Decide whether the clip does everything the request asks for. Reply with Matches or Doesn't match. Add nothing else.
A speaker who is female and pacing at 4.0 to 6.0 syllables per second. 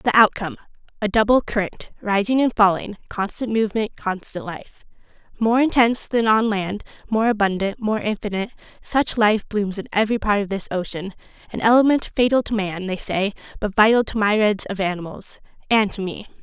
Matches